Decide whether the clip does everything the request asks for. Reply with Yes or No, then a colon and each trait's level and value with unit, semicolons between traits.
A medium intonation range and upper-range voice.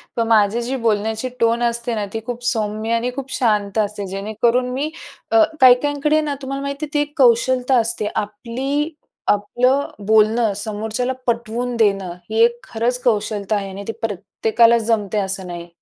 Yes: average, 3.0 semitones; high, 230 Hz